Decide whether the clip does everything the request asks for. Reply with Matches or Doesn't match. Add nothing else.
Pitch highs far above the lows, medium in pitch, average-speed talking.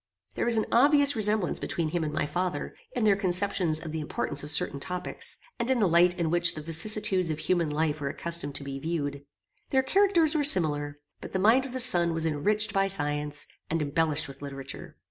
Doesn't match